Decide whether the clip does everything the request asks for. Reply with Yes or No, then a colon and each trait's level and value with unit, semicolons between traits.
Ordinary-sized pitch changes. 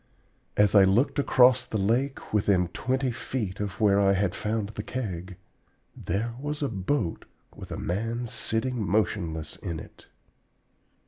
Yes: average, 4.3 semitones